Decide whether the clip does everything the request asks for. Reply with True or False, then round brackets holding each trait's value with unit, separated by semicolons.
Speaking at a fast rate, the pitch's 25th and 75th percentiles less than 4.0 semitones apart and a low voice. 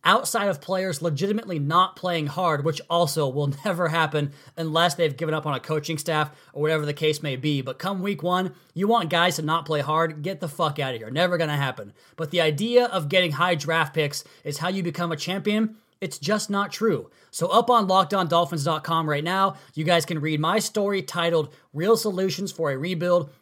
False (215 wpm; 3.6 semitones; 170 Hz)